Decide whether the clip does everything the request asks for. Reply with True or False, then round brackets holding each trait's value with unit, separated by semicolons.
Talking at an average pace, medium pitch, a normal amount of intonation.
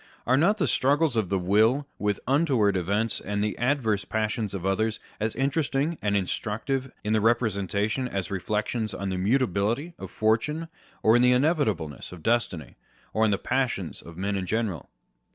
False (165 wpm; 110 Hz; 4.5 semitones)